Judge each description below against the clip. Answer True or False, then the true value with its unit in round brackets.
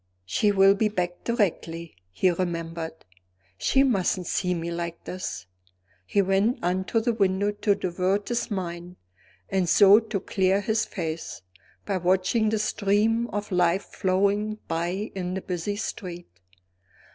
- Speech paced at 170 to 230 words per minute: False (145 wpm)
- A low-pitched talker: False (190 Hz)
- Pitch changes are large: False (2.9 semitones)